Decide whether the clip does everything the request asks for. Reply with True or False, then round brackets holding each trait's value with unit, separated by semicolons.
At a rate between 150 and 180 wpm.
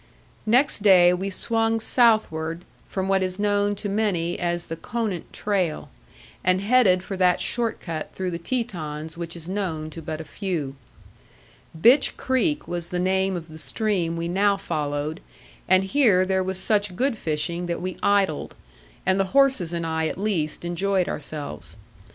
True (165 wpm)